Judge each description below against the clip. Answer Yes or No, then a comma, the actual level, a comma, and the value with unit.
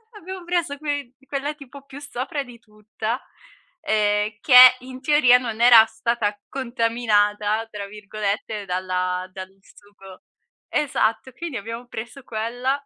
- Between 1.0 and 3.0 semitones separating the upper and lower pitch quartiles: No, average, 4.3 semitones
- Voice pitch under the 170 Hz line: No, high, 230 Hz